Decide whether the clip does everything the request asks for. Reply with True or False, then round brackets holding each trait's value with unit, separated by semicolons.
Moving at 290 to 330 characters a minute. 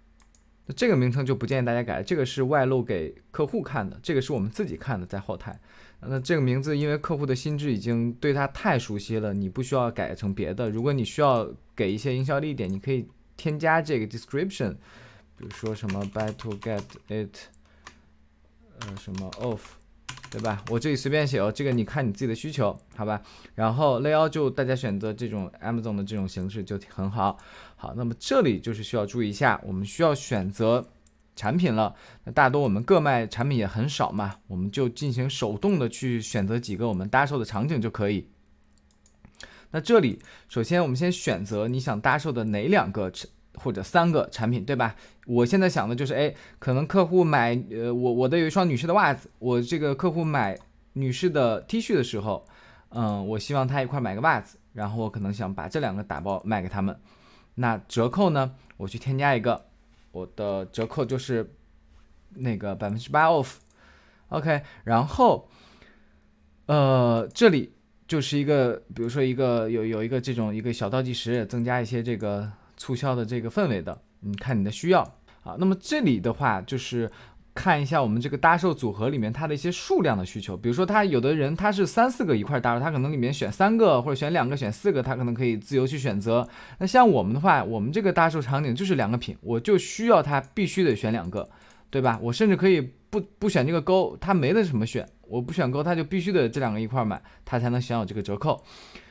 True (325 characters per minute)